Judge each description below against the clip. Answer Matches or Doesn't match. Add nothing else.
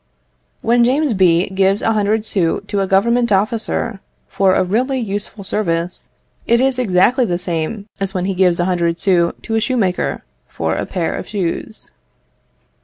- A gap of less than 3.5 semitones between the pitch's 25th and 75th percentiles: Doesn't match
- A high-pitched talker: Matches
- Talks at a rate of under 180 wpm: Matches